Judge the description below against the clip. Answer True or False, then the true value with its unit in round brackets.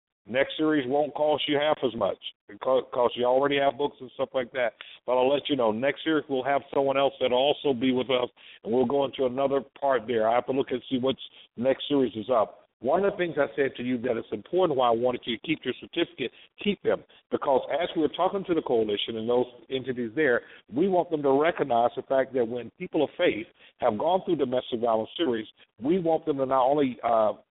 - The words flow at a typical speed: False (240 wpm)